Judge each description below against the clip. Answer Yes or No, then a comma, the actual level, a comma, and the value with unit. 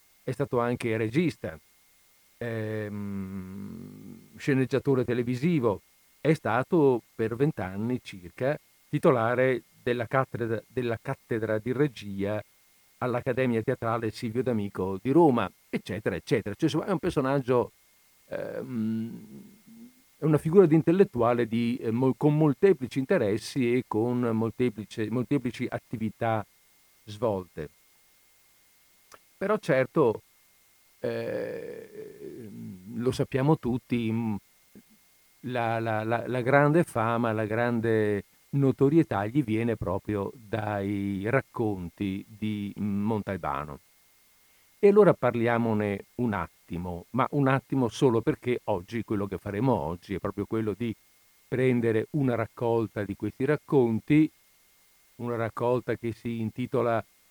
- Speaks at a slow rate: Yes, slow, 105 wpm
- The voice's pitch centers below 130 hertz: Yes, low, 120 Hz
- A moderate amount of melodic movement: Yes, average, 4.0 semitones